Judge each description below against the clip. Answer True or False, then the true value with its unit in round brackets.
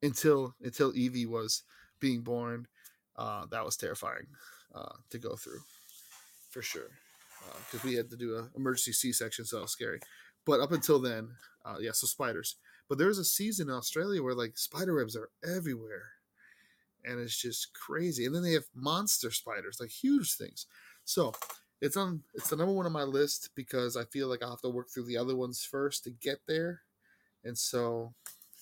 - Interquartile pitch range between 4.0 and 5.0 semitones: True (4.5 semitones)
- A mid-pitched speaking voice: False (125 Hz)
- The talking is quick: False (195 wpm)